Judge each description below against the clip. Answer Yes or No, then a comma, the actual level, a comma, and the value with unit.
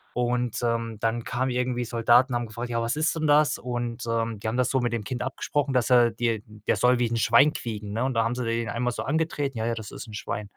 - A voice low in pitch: Yes, low, 120 Hz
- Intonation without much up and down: Yes, narrow, 1.7 semitones